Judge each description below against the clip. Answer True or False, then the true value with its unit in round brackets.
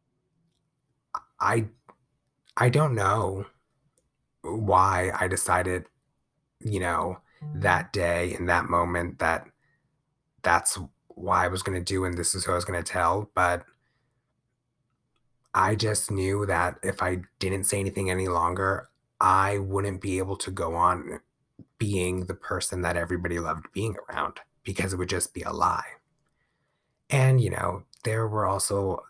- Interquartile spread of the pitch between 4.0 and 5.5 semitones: True (4.4 semitones)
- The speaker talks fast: False (140 wpm)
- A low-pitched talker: True (95 Hz)